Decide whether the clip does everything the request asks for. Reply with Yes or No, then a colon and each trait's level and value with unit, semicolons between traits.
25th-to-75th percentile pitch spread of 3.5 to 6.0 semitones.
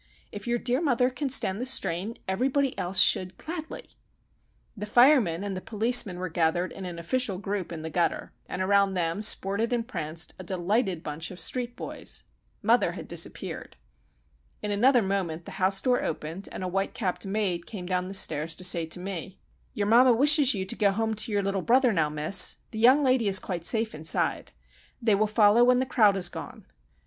Yes: average, 4.9 semitones